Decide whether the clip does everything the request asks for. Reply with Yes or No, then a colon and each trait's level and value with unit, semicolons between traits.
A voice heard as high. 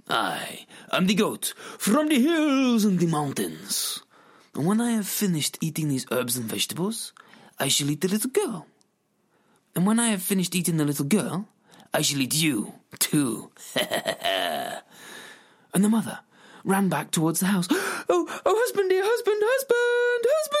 Yes: high, 210 Hz